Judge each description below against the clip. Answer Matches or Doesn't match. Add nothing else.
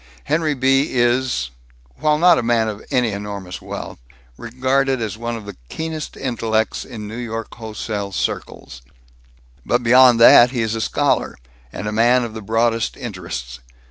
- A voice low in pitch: Matches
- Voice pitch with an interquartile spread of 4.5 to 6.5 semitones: Doesn't match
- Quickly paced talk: Doesn't match